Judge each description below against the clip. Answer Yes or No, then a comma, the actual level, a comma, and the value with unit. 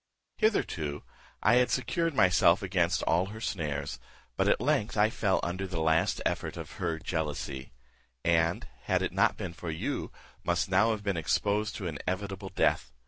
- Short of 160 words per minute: No, average, 165 wpm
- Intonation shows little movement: No, average, 4.0 semitones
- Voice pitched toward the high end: No, very low, 90 Hz